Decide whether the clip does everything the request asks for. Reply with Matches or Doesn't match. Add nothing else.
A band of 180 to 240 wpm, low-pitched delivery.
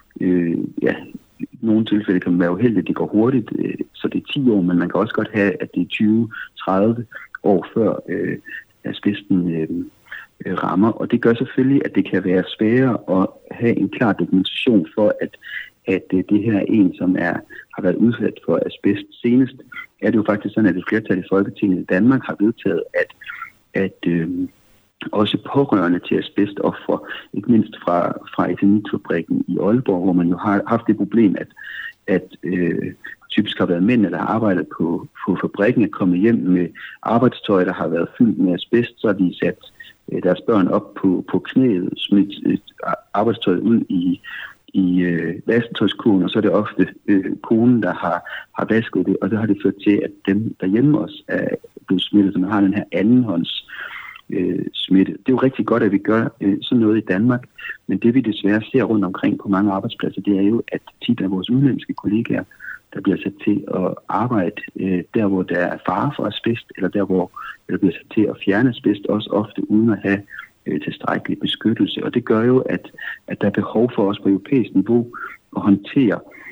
Matches